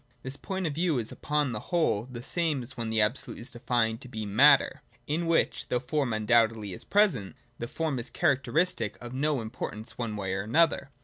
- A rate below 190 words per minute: No, fast, 205 wpm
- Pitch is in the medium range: No, low, 125 Hz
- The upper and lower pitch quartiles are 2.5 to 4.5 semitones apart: No, average, 5.1 semitones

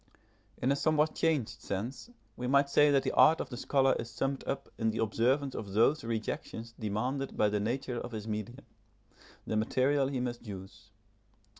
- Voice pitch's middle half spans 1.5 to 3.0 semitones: No, average, 4.0 semitones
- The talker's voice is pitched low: Yes, low, 125 Hz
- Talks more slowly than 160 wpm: No, average, 180 wpm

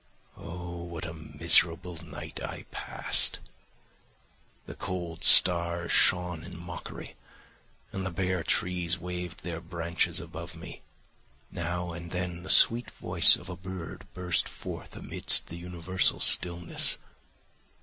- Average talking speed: No, slow, 125 wpm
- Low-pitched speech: Yes, very low, 85 Hz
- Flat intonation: Yes, narrow, 1.1 semitones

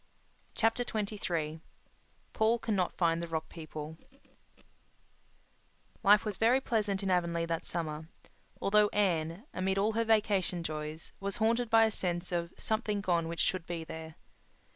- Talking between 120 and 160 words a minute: Yes, average, 140 wpm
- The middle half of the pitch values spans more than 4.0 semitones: Yes, average, 4.5 semitones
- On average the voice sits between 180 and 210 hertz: Yes, medium, 185 Hz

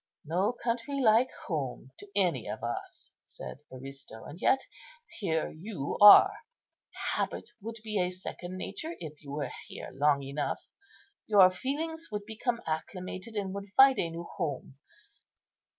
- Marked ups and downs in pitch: Yes, wide, 6.8 semitones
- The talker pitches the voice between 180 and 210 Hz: Yes, medium, 185 Hz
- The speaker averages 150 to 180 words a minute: No, average, 140 wpm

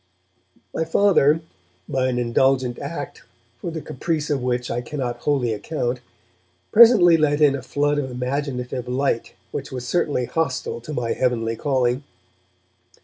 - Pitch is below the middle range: Yes, low, 130 Hz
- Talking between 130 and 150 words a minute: Yes, average, 145 wpm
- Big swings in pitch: No, average, 3.4 semitones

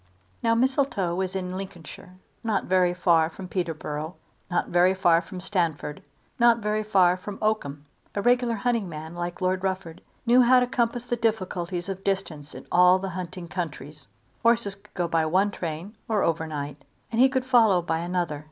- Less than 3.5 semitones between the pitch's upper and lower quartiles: No, average, 4.1 semitones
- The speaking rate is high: No, average, 170 wpm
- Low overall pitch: No, medium, 185 Hz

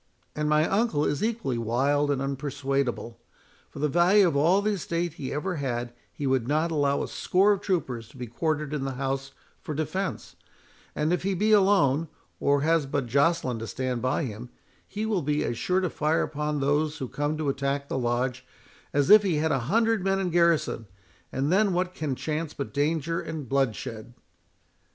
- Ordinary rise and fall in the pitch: Yes, average, 4.2 semitones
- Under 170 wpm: No, average, 190 wpm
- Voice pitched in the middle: Yes, medium, 150 Hz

